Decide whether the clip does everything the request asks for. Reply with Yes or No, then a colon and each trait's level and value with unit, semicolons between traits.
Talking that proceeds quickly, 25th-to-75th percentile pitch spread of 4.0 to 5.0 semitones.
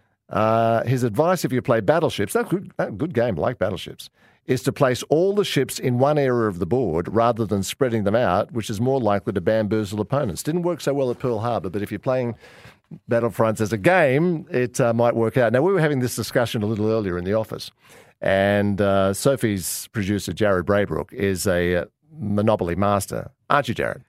Yes: fast, 210 wpm; average, 4.3 semitones